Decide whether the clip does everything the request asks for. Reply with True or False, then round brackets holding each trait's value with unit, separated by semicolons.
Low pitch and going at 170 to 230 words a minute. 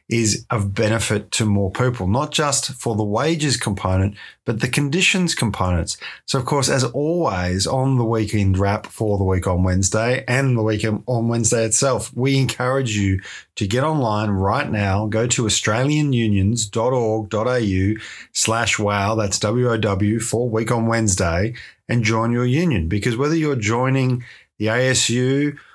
False (115 Hz; 150 wpm)